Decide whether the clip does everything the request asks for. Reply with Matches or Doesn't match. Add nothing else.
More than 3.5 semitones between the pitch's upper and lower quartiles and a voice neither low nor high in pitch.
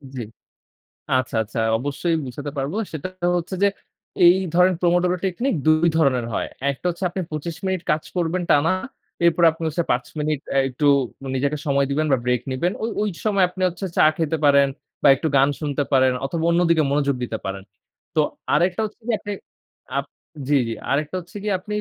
Matches